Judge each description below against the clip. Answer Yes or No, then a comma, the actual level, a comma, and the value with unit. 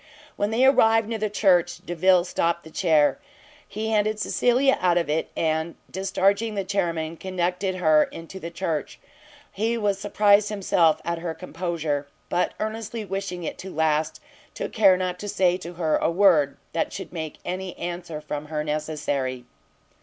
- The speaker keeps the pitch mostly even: No, average, 3.9 semitones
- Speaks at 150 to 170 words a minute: Yes, average, 165 wpm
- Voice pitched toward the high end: No, medium, 180 Hz